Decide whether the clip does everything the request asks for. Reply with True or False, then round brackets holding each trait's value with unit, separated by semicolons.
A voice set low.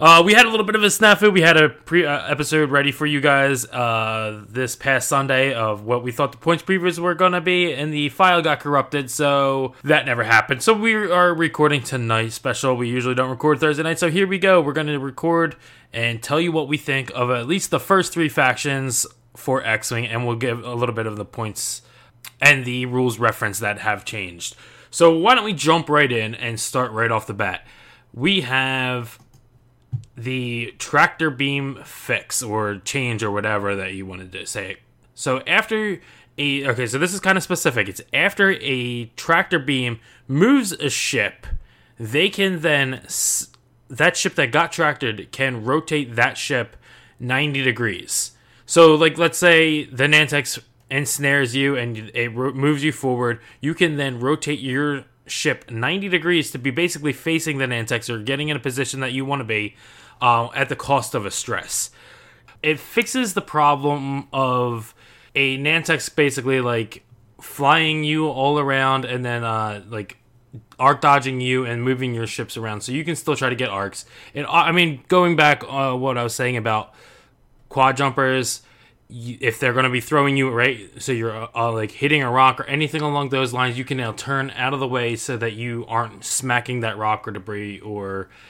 True (130 Hz)